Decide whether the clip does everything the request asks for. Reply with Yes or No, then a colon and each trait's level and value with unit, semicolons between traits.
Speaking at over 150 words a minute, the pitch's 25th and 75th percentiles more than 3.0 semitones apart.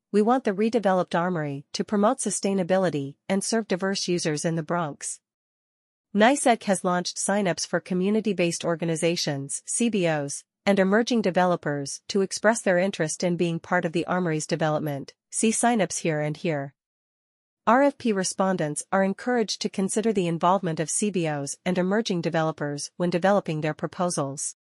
No: average, 145 wpm; average, 3.7 semitones